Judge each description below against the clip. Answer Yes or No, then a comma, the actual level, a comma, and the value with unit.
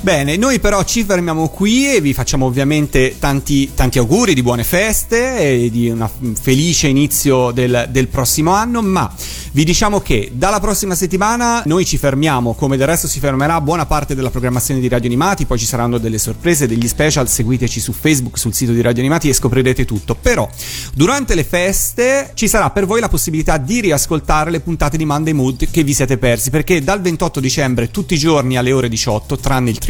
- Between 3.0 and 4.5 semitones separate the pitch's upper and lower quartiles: No, wide, 5.5 semitones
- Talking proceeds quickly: Yes, fast, 200 wpm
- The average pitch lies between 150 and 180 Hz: No, medium, 140 Hz